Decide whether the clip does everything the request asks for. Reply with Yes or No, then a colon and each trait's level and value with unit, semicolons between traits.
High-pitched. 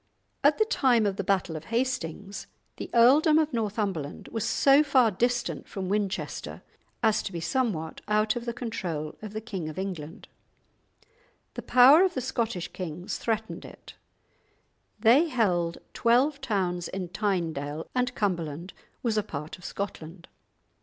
Yes: high, 210 Hz